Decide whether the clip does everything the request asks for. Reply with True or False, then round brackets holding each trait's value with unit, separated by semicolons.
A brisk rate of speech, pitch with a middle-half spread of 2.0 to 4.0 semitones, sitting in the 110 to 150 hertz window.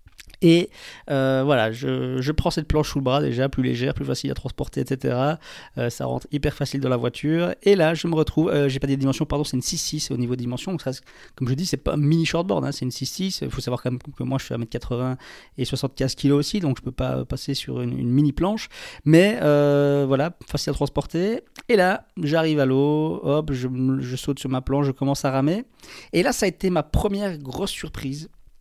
True (240 wpm; 3.3 semitones; 140 Hz)